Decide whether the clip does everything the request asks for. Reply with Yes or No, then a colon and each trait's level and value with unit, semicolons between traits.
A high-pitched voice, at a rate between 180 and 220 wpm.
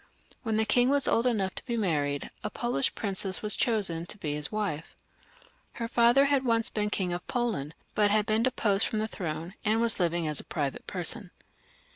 Yes: high, 210 Hz; average, 200 wpm